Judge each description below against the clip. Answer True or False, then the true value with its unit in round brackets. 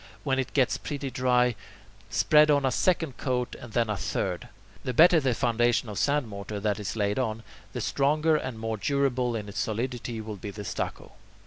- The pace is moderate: True (195 wpm)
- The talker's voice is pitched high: False (125 Hz)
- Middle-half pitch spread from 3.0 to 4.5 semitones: True (4.1 semitones)